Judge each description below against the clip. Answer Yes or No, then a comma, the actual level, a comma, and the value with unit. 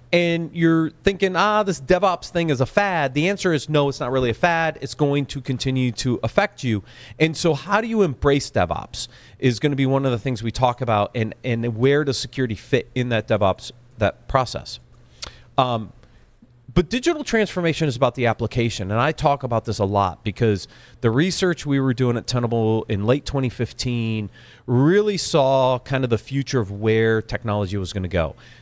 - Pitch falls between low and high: No, low, 130 Hz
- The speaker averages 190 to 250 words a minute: Yes, average, 195 wpm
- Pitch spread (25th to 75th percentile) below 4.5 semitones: No, wide, 5.4 semitones